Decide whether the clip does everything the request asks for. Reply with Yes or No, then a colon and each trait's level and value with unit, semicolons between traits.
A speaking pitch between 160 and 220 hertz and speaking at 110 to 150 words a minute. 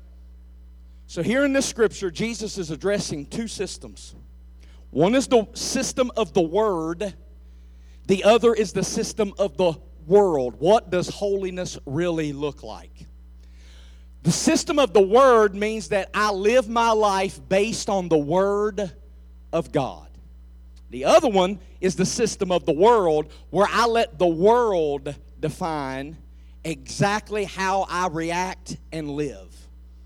Yes: medium, 185 Hz; average, 140 wpm